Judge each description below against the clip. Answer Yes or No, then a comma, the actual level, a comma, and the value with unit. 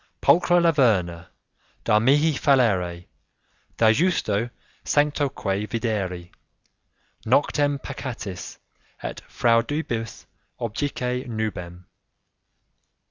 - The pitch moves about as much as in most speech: No, wide, 6.2 semitones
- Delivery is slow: Yes, slow, 70 wpm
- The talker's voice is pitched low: Yes, low, 115 Hz